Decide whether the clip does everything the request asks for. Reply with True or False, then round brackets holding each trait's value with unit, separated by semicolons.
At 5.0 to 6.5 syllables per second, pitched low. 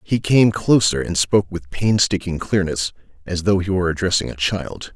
True (5.1 syllables/s; 95 Hz)